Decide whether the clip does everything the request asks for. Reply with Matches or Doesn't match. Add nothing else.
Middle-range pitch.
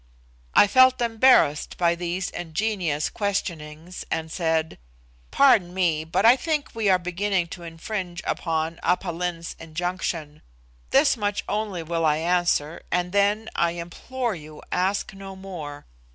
Matches